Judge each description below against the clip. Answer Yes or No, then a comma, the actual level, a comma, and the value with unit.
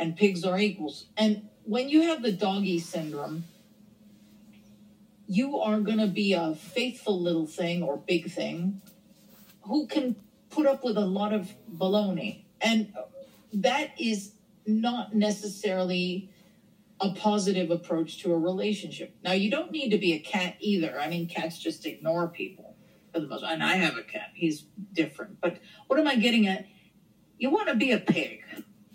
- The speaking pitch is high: Yes, high, 200 Hz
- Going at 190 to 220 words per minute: No, average, 165 wpm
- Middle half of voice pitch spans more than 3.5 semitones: No, average, 3.2 semitones